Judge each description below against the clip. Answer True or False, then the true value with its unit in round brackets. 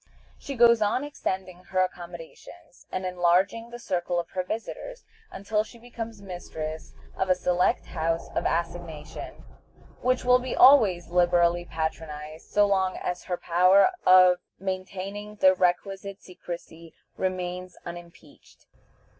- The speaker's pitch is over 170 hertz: True (185 Hz)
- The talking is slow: True (130 wpm)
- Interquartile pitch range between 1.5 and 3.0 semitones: True (2.6 semitones)